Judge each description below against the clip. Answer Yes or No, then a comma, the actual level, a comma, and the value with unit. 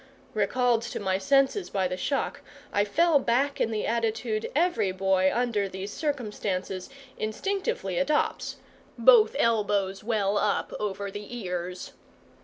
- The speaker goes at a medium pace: No, slow, 130 wpm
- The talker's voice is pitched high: Yes, high, 215 Hz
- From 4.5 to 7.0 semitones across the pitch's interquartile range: Yes, average, 5.0 semitones